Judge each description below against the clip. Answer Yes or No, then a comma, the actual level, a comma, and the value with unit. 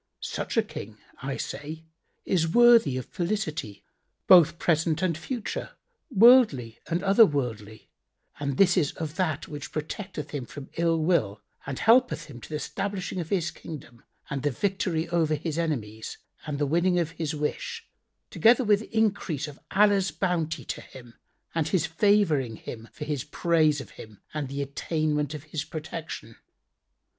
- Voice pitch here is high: No, medium, 160 Hz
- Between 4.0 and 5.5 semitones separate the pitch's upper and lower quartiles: Yes, average, 4.5 semitones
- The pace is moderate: Yes, average, 160 wpm